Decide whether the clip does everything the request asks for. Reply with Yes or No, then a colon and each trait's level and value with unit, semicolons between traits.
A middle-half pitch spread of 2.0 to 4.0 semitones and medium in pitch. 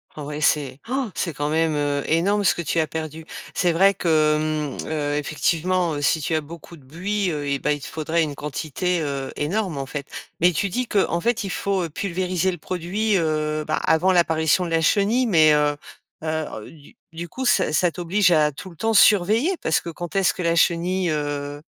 Yes: average, 3.5 semitones; medium, 165 Hz